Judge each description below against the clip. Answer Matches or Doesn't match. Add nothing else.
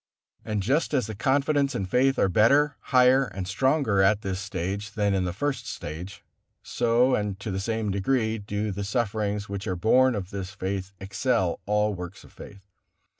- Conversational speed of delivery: Matches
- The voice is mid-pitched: Doesn't match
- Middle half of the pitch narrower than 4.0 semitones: Doesn't match